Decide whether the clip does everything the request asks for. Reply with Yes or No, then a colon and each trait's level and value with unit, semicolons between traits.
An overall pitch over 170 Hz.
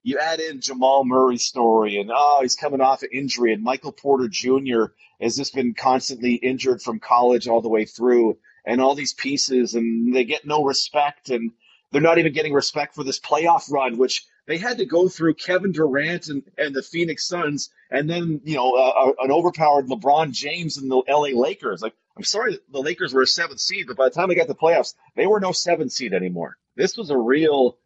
No: low, 135 Hz